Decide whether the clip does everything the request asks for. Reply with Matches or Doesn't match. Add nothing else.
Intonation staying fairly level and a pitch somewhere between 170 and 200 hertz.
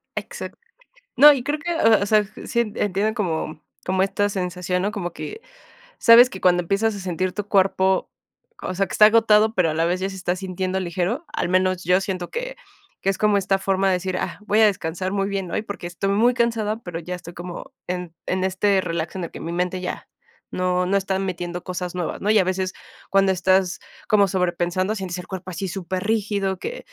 Matches